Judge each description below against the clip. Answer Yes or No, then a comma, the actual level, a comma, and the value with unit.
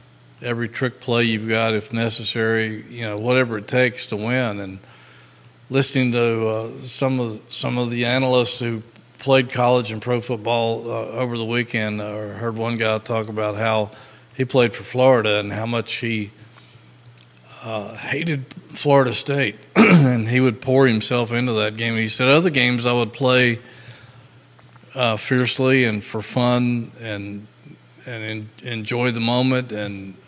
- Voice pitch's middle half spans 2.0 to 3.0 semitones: Yes, narrow, 2.5 semitones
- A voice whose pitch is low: Yes, low, 120 Hz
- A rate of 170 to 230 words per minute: No, average, 160 wpm